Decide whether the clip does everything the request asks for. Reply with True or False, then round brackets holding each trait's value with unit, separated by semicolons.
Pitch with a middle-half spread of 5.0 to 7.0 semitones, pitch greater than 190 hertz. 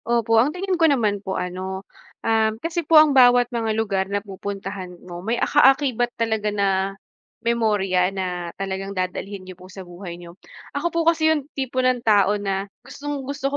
True (5.5 semitones; 220 Hz)